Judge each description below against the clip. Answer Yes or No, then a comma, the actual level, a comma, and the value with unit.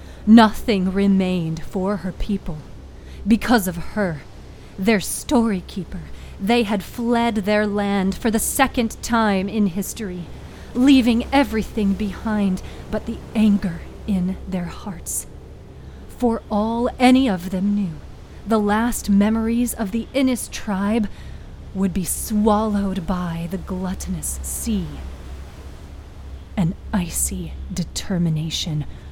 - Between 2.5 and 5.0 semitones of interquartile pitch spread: Yes, average, 4.1 semitones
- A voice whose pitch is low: No, high, 200 Hz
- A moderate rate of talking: No, slow, 110 wpm